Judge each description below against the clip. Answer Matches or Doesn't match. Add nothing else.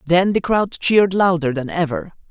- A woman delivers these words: Doesn't match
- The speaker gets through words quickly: Doesn't match